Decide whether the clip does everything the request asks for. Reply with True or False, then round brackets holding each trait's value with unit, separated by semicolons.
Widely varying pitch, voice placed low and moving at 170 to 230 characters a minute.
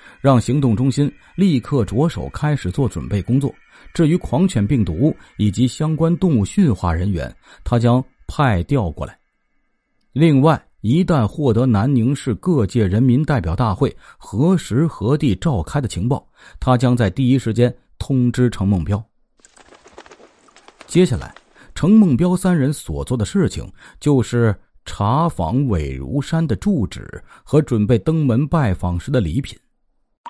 True (6.4 semitones; 125 Hz; 220 characters per minute)